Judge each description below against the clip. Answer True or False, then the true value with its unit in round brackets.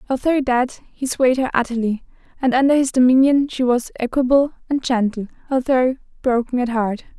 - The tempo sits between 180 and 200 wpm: False (160 wpm)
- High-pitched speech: True (255 Hz)